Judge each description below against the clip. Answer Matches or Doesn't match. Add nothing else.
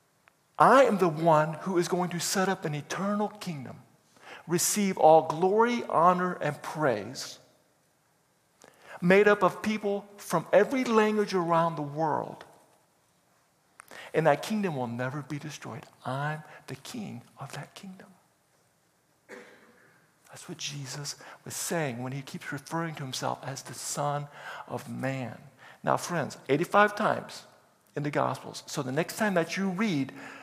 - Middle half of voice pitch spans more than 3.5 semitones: Matches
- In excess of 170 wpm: Doesn't match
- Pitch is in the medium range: Matches